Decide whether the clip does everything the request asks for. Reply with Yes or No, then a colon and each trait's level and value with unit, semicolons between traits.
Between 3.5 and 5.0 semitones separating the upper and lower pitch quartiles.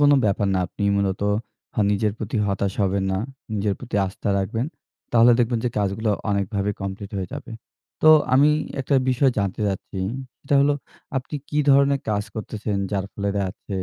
Yes: average, 4.0 semitones